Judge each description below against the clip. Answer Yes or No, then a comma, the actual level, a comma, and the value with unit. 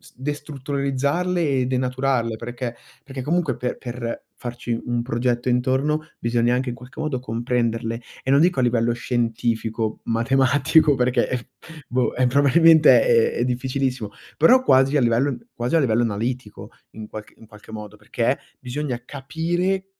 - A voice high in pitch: No, low, 125 Hz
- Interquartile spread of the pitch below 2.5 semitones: No, average, 2.9 semitones